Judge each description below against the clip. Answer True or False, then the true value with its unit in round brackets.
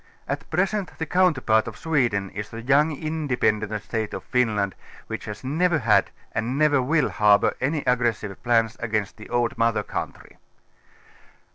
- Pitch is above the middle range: False (120 Hz)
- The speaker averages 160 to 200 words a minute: False (150 wpm)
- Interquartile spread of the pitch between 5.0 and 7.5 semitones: True (5.6 semitones)